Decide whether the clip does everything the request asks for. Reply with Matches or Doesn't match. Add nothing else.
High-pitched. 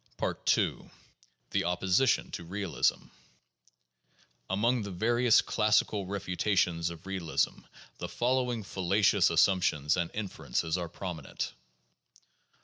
Doesn't match